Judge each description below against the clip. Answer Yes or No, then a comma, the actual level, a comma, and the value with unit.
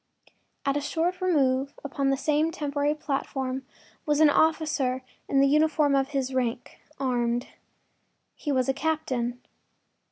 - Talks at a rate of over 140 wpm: No, slow, 135 wpm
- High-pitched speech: Yes, very high, 275 Hz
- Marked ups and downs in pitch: No, narrow, 2.6 semitones